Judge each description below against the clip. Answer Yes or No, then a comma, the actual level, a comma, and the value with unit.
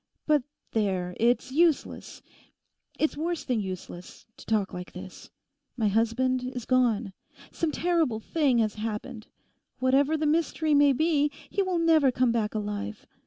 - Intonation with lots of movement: Yes, wide, 6.1 semitones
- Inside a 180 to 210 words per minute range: No, average, 145 wpm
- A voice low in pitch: No, very high, 255 Hz